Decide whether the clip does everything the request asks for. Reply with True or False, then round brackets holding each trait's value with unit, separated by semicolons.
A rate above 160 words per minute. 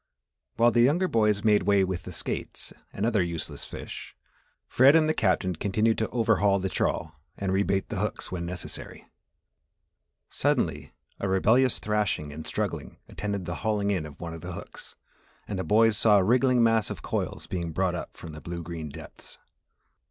True (180 wpm)